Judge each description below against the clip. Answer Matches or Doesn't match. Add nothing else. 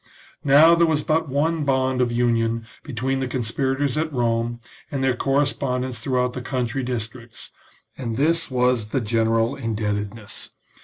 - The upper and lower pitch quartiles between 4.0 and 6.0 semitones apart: Doesn't match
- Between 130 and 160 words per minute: Matches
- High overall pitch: Doesn't match